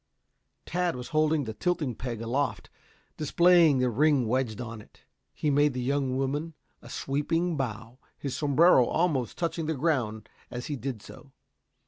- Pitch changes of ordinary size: Yes, average, 4.2 semitones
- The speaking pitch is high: No, medium, 140 Hz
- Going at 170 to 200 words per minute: No, average, 155 wpm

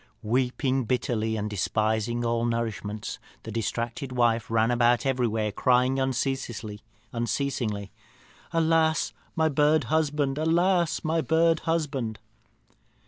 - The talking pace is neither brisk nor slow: No, slow, 100 wpm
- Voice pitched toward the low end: Yes, low, 125 Hz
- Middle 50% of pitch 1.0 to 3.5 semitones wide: No, average, 4.8 semitones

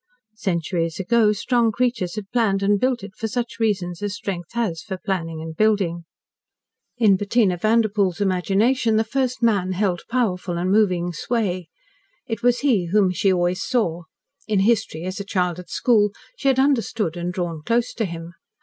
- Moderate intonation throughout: Yes, average, 4.3 semitones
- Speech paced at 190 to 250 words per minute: No, average, 175 wpm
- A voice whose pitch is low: No, high, 200 Hz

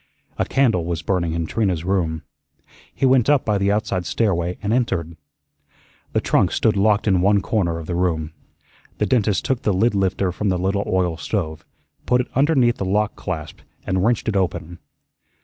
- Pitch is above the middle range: No, very low, 95 Hz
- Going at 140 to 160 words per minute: No, average, 185 wpm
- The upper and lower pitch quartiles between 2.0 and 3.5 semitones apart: No, average, 3.9 semitones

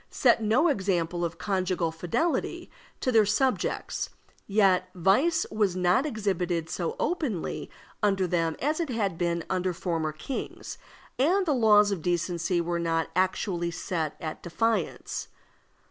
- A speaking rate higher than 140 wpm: No, slow, 135 wpm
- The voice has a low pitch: No, medium, 185 Hz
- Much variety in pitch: No, average, 4.5 semitones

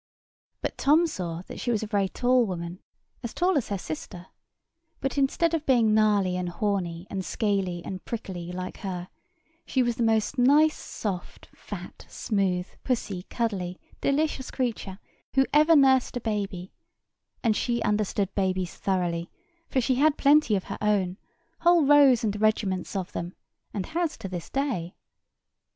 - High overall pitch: Yes, high, 210 Hz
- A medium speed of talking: Yes, average, 160 wpm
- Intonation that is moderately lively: No, wide, 6.1 semitones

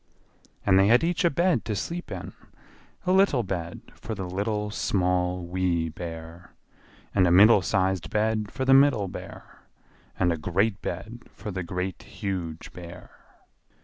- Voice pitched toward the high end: No, very low, 95 Hz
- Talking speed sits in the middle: Yes, average, 155 wpm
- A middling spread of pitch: Yes, average, 3.8 semitones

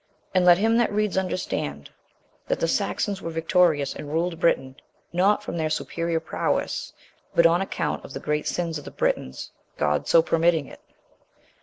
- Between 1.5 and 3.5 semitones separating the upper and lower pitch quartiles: Yes, average, 2.8 semitones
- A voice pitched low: No, medium, 170 Hz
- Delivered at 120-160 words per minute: No, average, 170 wpm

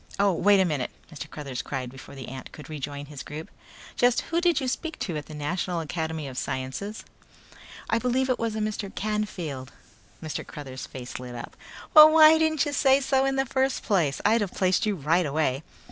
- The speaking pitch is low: No, medium, 175 Hz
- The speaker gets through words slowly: No, fast, 205 wpm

